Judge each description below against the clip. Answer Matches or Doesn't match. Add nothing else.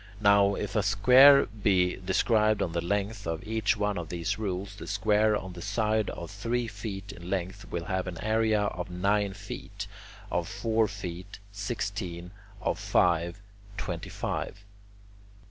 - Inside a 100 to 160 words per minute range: Matches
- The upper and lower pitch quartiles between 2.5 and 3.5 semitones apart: Matches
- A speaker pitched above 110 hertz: Doesn't match